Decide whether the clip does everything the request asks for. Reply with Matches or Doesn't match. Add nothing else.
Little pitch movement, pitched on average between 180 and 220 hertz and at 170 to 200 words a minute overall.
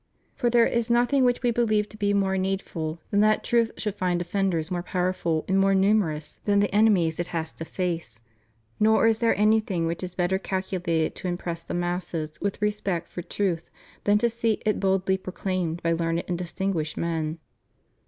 Doesn't match